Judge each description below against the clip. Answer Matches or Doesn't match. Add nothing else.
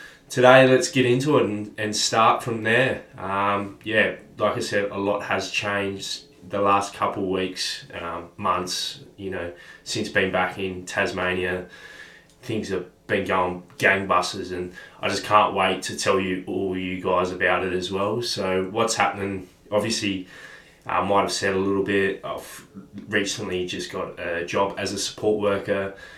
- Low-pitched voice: Matches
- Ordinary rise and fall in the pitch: Doesn't match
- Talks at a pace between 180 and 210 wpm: Doesn't match